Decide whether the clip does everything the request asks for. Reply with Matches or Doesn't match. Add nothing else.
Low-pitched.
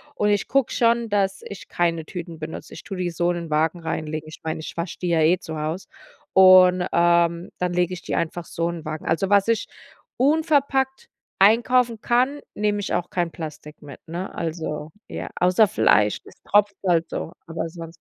Doesn't match